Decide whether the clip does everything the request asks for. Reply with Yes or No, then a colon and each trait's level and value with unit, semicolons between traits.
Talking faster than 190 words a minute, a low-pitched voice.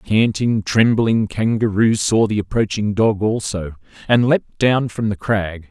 No: average, 160 wpm; low, 105 Hz